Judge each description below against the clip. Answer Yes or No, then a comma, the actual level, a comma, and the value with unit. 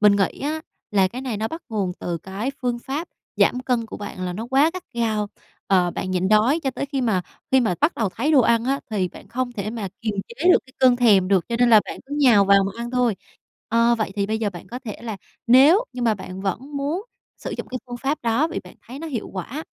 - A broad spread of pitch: No, average, 4.7 semitones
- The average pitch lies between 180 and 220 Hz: No, high, 235 Hz